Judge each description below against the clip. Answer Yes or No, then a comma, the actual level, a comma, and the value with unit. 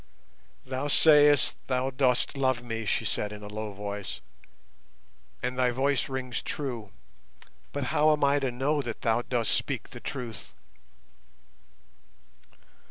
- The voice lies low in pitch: Yes, low, 125 Hz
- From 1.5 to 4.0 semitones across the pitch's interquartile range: Yes, average, 3.4 semitones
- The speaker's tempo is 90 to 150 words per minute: Yes, slow, 135 wpm